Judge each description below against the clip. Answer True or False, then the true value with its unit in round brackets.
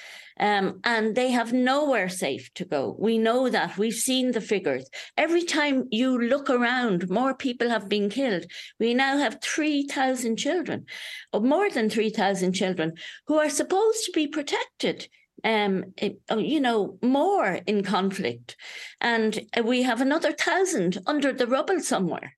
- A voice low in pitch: False (240 Hz)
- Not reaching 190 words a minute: True (150 wpm)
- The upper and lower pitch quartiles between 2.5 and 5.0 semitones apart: False (5.6 semitones)